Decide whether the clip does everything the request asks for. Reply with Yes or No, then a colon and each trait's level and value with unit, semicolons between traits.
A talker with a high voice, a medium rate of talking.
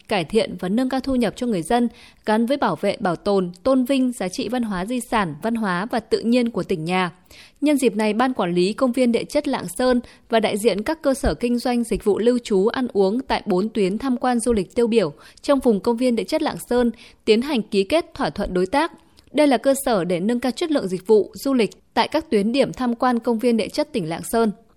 No: high, 235 Hz; fast, 265 wpm